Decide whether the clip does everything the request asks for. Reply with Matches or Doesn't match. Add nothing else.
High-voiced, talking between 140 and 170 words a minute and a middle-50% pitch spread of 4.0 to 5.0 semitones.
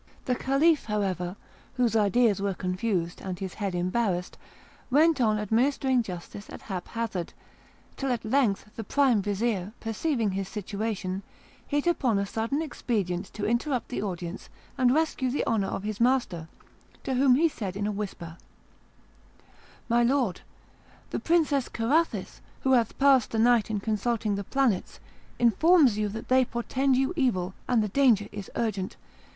Matches